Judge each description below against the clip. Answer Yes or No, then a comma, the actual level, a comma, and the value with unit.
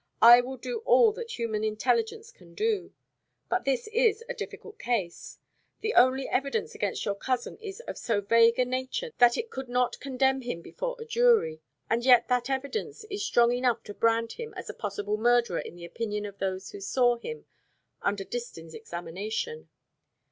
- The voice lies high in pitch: Yes, very high, 250 Hz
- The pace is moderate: Yes, average, 180 wpm